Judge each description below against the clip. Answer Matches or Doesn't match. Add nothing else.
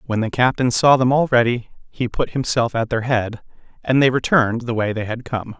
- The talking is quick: Matches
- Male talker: Matches